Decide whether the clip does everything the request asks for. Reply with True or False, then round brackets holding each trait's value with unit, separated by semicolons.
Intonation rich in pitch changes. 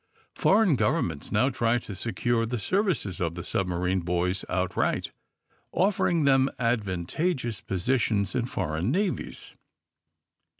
True (6.6 semitones)